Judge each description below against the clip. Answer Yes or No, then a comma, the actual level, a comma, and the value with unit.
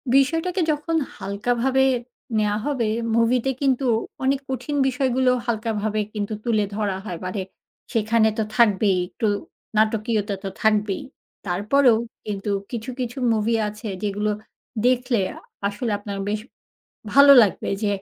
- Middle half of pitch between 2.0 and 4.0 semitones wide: Yes, average, 3.6 semitones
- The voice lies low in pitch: No, high, 225 Hz